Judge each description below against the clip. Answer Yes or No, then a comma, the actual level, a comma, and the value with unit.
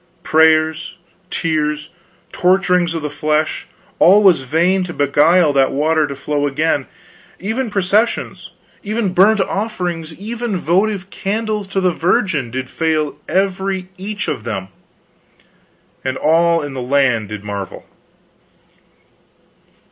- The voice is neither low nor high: Yes, medium, 165 Hz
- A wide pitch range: No, average, 4.7 semitones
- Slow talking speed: Yes, slow, 120 wpm